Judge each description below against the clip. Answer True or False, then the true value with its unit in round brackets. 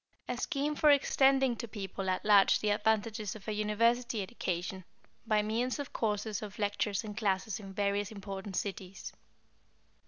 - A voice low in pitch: False (210 Hz)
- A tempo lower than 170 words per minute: True (160 wpm)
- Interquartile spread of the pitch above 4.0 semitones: False (2.7 semitones)